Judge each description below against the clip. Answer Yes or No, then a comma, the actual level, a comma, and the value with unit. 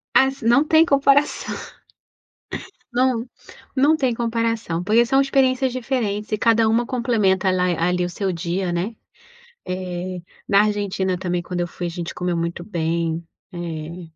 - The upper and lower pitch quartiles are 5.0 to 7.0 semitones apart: Yes, wide, 5.4 semitones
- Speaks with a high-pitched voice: Yes, high, 200 Hz